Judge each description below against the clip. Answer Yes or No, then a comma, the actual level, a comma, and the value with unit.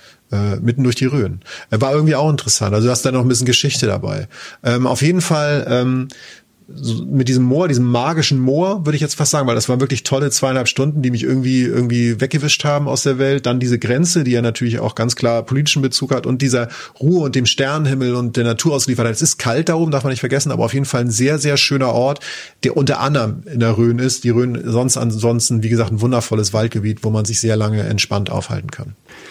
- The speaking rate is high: Yes, fast, 235 wpm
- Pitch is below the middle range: Yes, low, 125 Hz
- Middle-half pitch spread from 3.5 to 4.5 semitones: No, average, 3.1 semitones